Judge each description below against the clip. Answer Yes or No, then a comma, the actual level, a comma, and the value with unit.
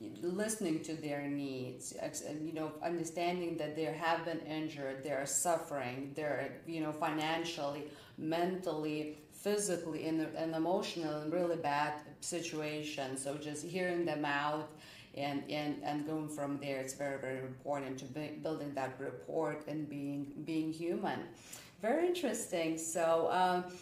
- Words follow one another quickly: No, average, 145 wpm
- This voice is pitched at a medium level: Yes, medium, 155 Hz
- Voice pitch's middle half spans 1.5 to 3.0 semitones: Yes, narrow, 2.5 semitones